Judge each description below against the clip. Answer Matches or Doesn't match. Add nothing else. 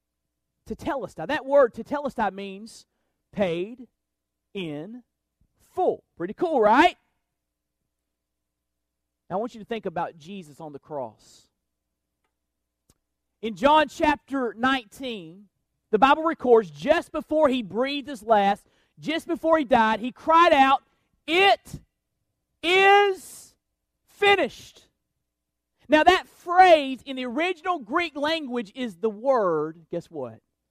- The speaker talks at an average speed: Doesn't match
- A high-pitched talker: Matches